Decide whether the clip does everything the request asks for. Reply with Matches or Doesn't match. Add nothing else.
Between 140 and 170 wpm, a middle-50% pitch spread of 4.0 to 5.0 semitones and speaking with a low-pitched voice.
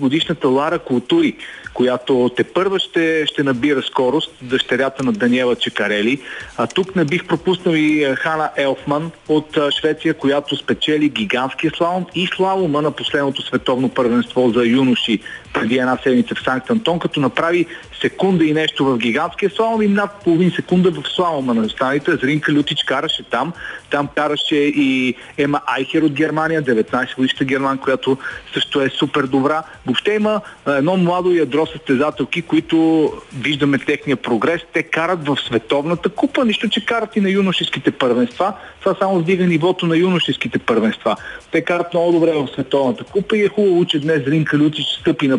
Doesn't match